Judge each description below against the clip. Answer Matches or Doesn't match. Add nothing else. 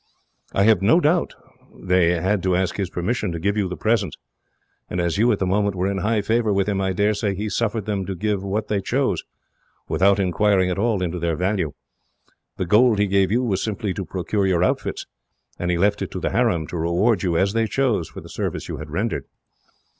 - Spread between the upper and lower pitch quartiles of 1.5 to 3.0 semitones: Matches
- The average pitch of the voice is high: Doesn't match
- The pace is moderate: Doesn't match